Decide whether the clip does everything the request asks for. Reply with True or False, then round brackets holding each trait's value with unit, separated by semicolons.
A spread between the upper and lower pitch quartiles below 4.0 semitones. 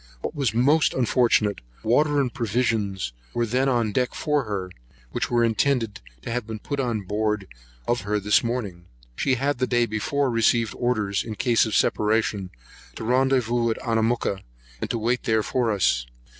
True (3.0 semitones)